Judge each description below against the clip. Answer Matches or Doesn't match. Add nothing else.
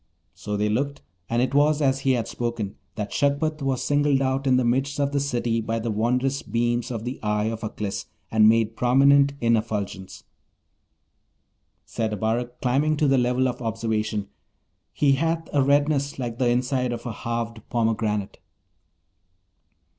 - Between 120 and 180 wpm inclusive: Matches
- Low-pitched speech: Matches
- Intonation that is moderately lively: Matches